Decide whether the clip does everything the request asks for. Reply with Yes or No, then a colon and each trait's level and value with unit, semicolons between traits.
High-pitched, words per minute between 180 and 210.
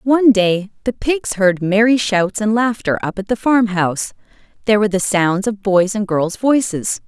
Yes: high, 210 Hz; average, 185 wpm